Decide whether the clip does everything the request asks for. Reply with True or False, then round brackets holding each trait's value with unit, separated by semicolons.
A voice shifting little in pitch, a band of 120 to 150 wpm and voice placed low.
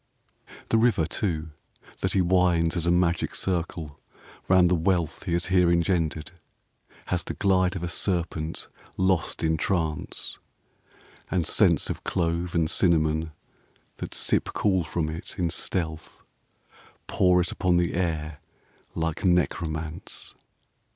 True (2.1 semitones; 135 wpm; 85 Hz)